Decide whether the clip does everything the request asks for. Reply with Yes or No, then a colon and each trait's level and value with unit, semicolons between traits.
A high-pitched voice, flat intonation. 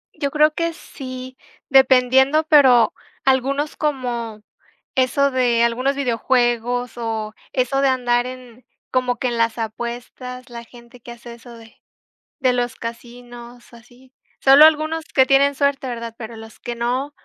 Yes: very high, 250 Hz; narrow, 2.2 semitones